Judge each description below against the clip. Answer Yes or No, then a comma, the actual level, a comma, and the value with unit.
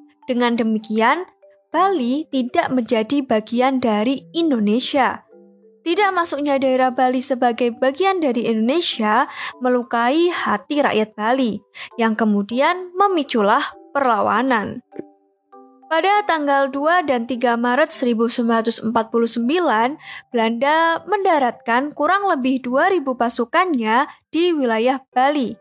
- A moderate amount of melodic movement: Yes, average, 4.7 semitones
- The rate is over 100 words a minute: No, average, 95 wpm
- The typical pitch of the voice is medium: No, very high, 260 Hz